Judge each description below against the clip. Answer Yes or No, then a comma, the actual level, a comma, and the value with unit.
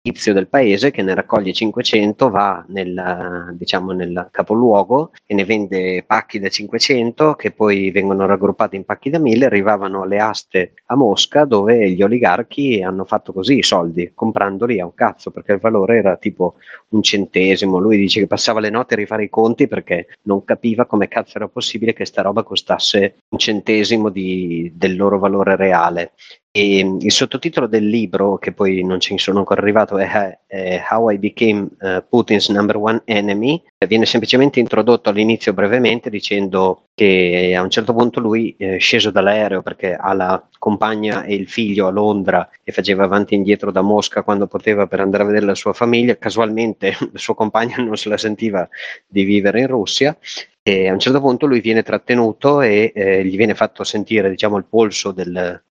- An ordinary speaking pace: No, fast, 180 wpm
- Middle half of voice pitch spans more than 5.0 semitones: No, narrow, 2.6 semitones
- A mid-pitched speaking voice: No, low, 105 Hz